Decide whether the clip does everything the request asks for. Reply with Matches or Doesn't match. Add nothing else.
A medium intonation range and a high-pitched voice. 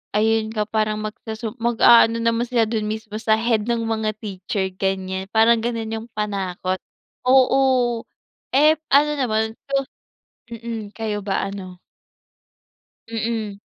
Doesn't match